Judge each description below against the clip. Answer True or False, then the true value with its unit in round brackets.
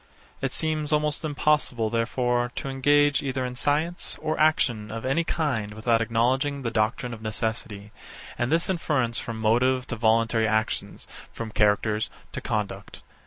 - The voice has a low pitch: True (120 Hz)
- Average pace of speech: True (150 wpm)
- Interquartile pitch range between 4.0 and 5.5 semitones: True (4.6 semitones)